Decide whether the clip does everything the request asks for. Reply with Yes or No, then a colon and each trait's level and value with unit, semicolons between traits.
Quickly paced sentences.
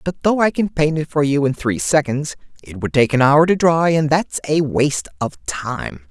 Yes: fast, 235 wpm